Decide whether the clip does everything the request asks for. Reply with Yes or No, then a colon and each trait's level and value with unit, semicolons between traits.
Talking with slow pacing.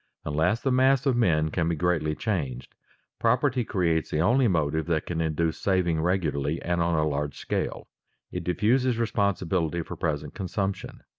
No: average, 160 wpm